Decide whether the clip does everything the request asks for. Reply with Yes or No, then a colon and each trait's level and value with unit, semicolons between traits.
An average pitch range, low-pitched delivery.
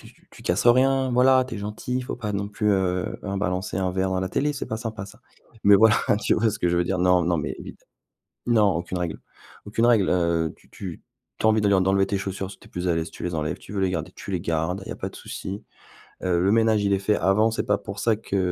Yes: average, 3.2 semitones; low, 100 Hz